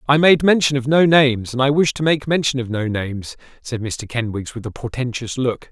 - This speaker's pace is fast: Yes, fast, 230 wpm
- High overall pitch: No, low, 130 Hz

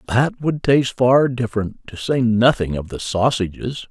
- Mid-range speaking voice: No, low, 120 Hz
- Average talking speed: Yes, average, 170 wpm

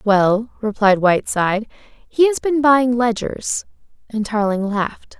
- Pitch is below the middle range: No, high, 225 Hz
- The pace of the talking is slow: Yes, slow, 125 wpm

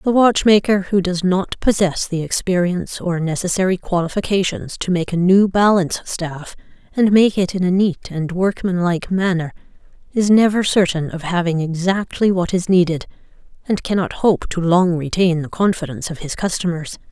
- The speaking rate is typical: Yes, average, 160 wpm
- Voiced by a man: No, female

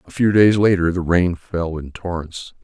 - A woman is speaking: No, male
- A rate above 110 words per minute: Yes, fast, 205 wpm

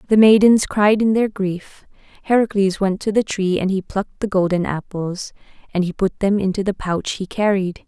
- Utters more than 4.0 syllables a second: Yes, 5.0 syllables/s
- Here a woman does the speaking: Yes, female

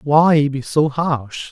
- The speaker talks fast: No, average, 160 wpm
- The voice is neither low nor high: Yes, medium, 145 Hz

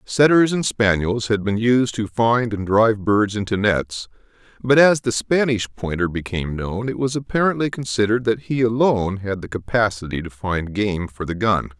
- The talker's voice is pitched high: No, low, 110 Hz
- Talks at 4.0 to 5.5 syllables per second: Yes, 5.0 syllables/s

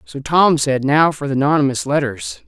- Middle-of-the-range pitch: Yes, medium, 145 Hz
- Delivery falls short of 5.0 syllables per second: Yes, 4.7 syllables/s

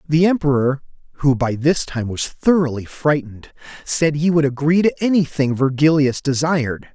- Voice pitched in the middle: Yes, medium, 145 Hz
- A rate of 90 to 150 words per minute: Yes, average, 145 wpm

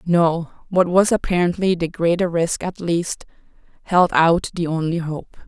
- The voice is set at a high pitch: No, medium, 170 Hz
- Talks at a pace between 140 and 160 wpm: Yes, average, 155 wpm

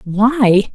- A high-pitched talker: Yes, high, 220 Hz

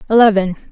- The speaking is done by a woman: Yes, female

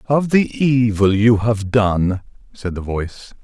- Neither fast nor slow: Yes, average, 155 wpm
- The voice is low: Yes, low, 110 Hz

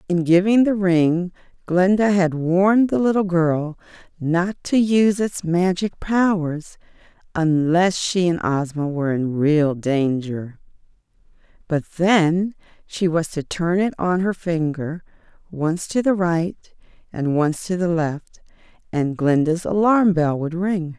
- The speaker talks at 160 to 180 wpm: No, average, 140 wpm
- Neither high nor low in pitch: Yes, medium, 175 Hz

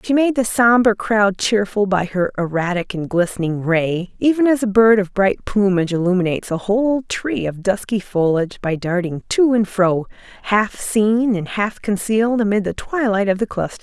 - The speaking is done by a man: No, female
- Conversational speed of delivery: Yes, average, 185 wpm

